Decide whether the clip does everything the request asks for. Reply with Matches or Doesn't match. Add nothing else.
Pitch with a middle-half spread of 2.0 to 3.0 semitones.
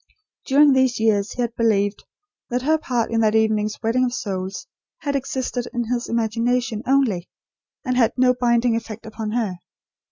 Matches